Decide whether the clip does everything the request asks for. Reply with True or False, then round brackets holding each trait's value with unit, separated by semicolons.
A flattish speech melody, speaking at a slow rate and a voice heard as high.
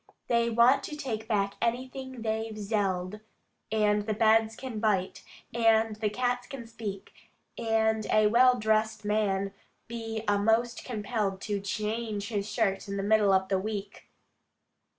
False (2.1 semitones; 145 wpm; 220 Hz)